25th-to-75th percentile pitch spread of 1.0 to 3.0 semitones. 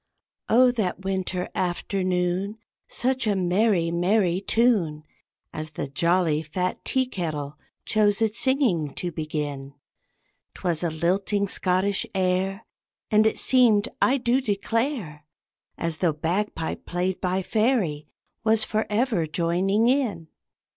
No: average, 4.5 semitones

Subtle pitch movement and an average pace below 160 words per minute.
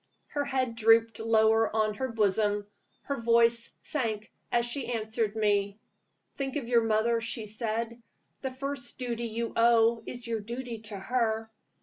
Yes: narrow, 1.6 semitones; average, 150 wpm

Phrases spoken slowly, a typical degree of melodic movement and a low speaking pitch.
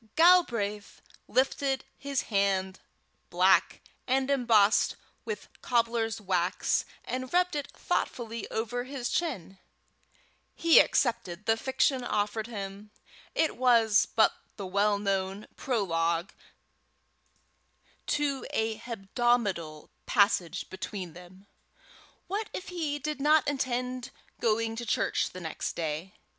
No: slow, 110 wpm; average, 5.0 semitones; high, 225 Hz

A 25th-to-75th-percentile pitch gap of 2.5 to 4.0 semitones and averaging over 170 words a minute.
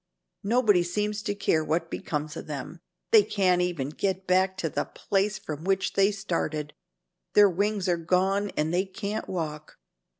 No: average, 3.5 semitones; average, 165 wpm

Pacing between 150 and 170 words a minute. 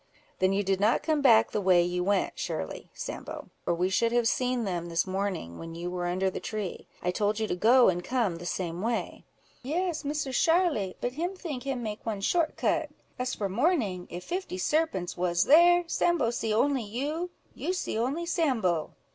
No: average, 195 wpm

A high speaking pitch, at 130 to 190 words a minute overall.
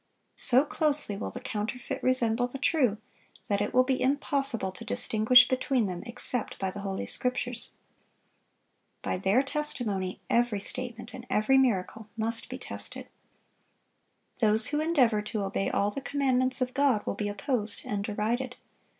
Yes: high, 240 Hz; average, 150 wpm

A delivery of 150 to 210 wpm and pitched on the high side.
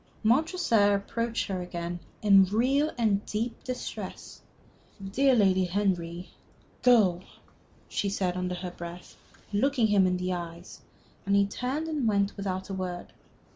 No: average, 140 wpm; high, 200 Hz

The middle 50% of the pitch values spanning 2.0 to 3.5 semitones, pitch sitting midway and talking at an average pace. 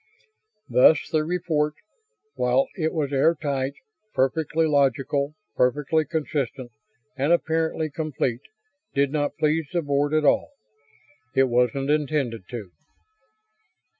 No: average, 2.7 semitones; medium, 145 Hz; slow, 110 wpm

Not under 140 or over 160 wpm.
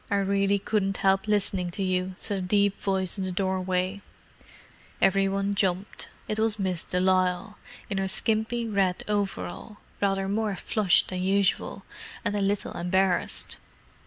Yes: average, 150 wpm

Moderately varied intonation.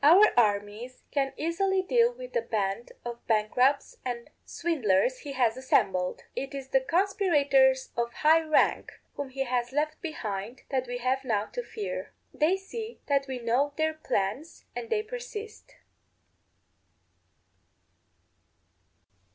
No: wide, 5.9 semitones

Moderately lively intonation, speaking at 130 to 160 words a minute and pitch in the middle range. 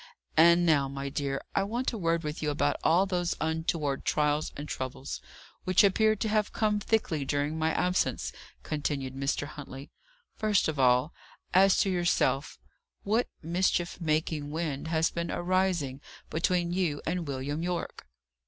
Yes: average, 4.1 semitones; average, 155 wpm; medium, 160 Hz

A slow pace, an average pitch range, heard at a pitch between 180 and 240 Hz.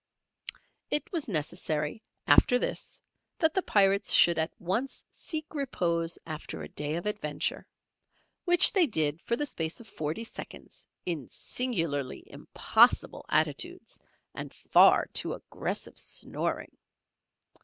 No: slow, 120 wpm; wide, 8.1 semitones; medium, 185 Hz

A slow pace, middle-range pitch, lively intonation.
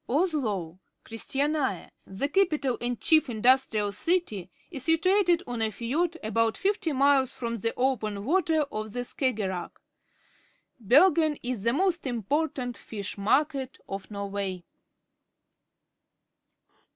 No: slow, 115 wpm; very high, 255 Hz; wide, 6.3 semitones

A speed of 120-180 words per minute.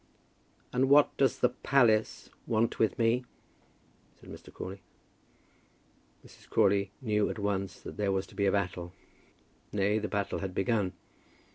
Yes: average, 145 wpm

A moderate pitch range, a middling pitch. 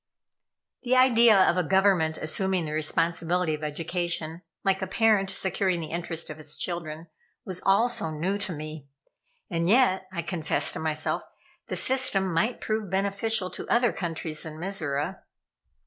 Yes: average, 3.6 semitones; medium, 180 Hz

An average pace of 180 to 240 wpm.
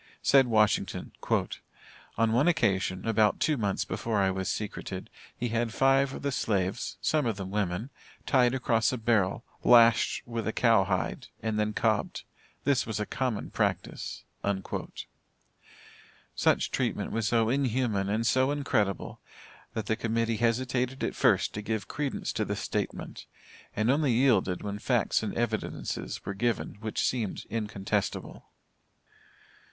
No: average, 145 wpm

